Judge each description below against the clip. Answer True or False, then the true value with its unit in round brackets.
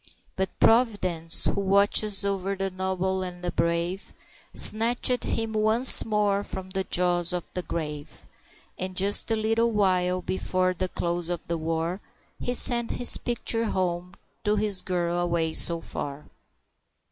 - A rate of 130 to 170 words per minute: True (145 wpm)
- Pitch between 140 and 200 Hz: True (185 Hz)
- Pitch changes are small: False (3.2 semitones)